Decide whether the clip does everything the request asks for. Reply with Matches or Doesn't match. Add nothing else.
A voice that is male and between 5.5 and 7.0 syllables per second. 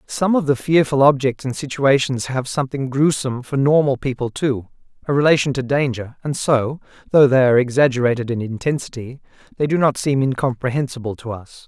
Matches